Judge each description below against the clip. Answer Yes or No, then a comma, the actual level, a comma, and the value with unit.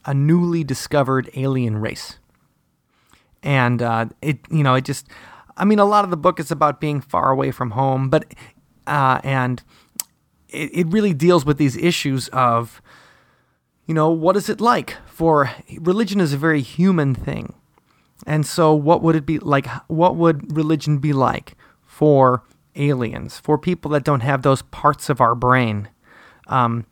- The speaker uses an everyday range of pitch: Yes, average, 3.9 semitones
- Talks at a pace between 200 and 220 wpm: No, average, 165 wpm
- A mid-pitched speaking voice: Yes, medium, 145 Hz